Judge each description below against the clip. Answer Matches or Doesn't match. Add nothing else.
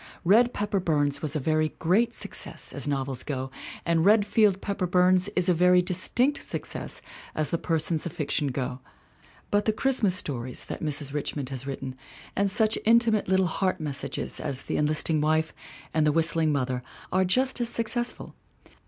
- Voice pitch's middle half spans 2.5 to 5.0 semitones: Doesn't match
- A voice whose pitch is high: Doesn't match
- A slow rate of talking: Doesn't match